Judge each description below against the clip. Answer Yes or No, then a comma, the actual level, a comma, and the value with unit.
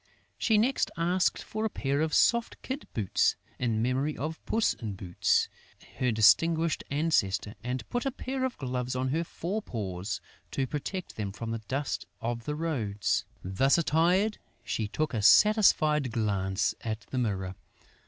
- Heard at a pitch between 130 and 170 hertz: Yes, low, 135 Hz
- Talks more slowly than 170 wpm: Yes, average, 160 wpm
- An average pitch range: No, wide, 7.4 semitones